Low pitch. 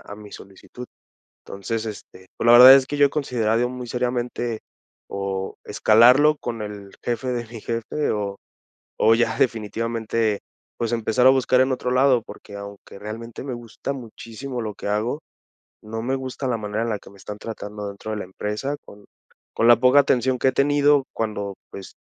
Yes: low, 115 Hz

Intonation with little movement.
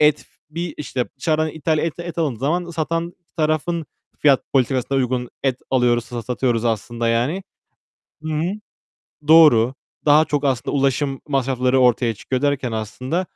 No: average, 4.2 semitones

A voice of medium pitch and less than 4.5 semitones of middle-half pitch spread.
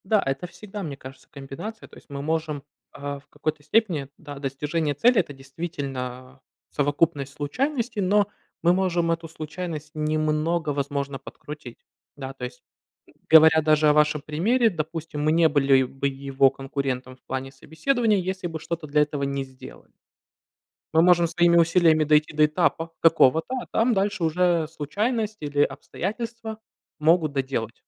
Yes: medium, 155 Hz; average, 3.7 semitones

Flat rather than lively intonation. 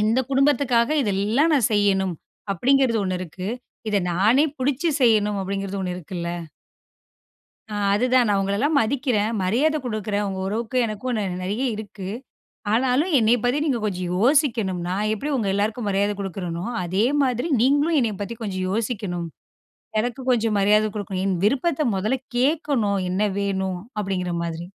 No: average, 4.5 semitones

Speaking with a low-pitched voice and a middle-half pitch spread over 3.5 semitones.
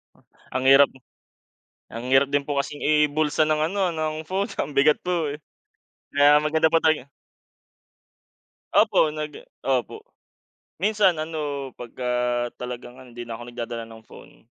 No: medium, 145 Hz; average, 4.0 semitones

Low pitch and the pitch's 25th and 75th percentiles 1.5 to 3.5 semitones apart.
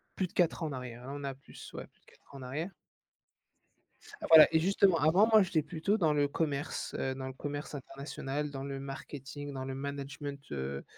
No: medium, 145 Hz; average, 2.8 semitones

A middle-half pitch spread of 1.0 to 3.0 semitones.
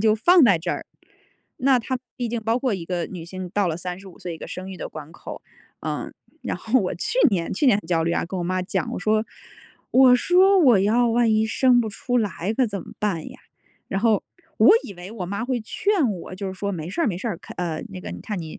No: average, 5.1 semitones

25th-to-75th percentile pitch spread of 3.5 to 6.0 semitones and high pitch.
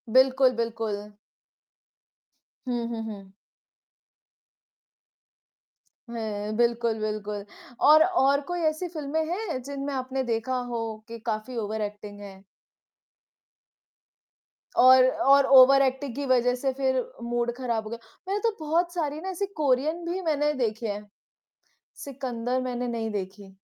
Yes: average, 4.0 semitones; very high, 250 Hz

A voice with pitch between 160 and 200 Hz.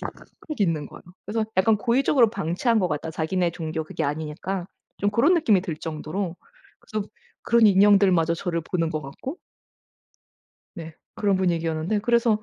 Yes: medium, 185 Hz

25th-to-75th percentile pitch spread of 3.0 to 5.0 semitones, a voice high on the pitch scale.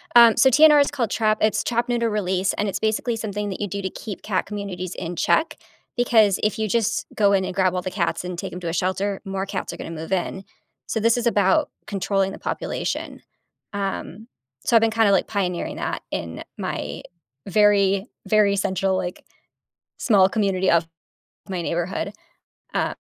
No: narrow, 2.6 semitones; high, 200 Hz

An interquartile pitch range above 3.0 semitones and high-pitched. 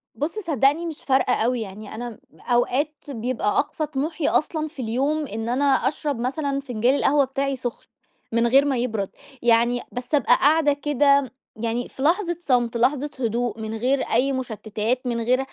Yes: average, 3.5 semitones; very high, 260 Hz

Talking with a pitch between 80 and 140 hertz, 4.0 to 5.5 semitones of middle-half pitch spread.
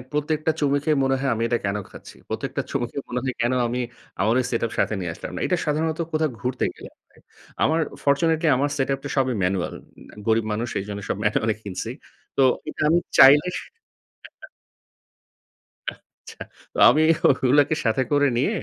Yes: low, 135 Hz; average, 4.5 semitones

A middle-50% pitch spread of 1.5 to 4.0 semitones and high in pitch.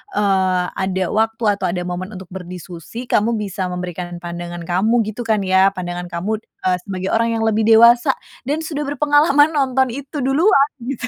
No: wide, 5.6 semitones; high, 210 Hz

